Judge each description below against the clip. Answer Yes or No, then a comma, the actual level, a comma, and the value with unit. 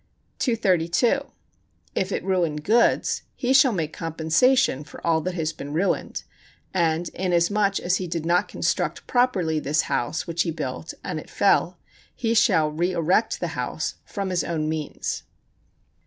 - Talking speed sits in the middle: Yes, average, 150 wpm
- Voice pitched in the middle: Yes, medium, 175 Hz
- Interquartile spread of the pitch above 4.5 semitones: No, average, 3.9 semitones